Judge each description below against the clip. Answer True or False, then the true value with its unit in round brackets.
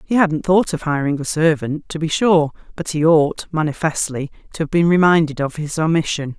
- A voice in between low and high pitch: True (160 Hz)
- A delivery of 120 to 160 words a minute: False (195 wpm)